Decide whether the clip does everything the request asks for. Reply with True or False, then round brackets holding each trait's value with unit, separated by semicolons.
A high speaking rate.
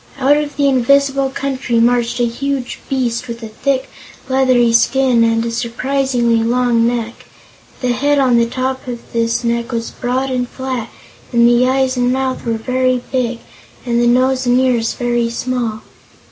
False (170 wpm)